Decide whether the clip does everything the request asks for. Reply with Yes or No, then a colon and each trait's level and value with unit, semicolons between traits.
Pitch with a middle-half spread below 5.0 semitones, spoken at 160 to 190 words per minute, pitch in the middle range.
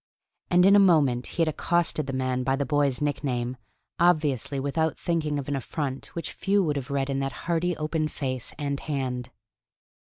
Yes: average, 3.4 semitones; average, 185 wpm; medium, 145 Hz